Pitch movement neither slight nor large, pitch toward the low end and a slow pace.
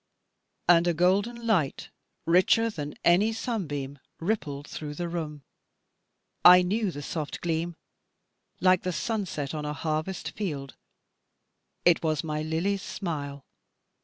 No: average, 4.2 semitones; medium, 170 Hz; slow, 125 wpm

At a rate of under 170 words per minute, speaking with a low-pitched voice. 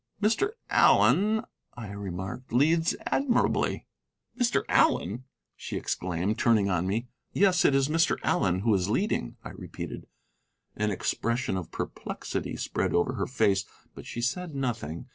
Yes: average, 140 wpm; low, 115 Hz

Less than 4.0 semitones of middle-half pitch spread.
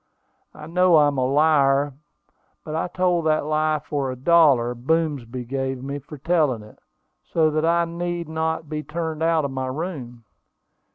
Yes: average, 3.4 semitones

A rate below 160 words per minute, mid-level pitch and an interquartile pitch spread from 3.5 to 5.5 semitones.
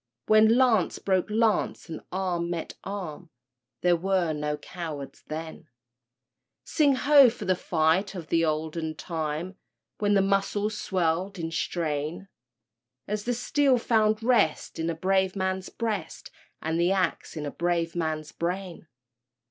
Yes: average, 140 wpm; medium, 180 Hz; average, 4.1 semitones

